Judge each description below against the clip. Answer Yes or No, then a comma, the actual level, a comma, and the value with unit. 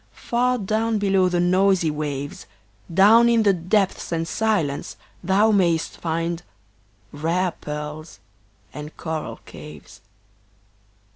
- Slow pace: Yes, slow, 110 wpm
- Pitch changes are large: No, average, 4.6 semitones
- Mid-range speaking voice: Yes, medium, 175 Hz